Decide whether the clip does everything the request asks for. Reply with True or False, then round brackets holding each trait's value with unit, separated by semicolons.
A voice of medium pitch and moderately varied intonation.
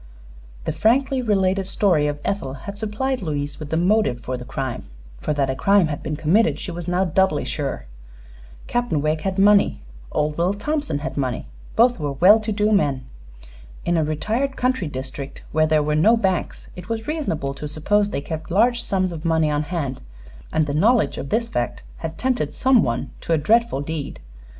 False (170 Hz; 6.3 semitones)